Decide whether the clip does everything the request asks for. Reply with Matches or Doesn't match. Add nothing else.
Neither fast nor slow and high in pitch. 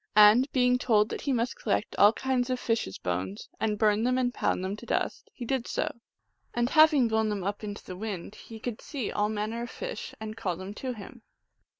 Doesn't match